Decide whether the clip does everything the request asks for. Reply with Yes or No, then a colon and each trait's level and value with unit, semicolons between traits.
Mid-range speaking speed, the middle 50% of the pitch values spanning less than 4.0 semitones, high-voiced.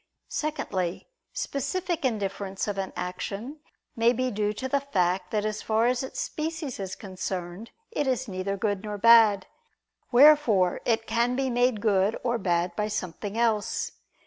No: average, 155 wpm; average, 4.5 semitones; high, 220 Hz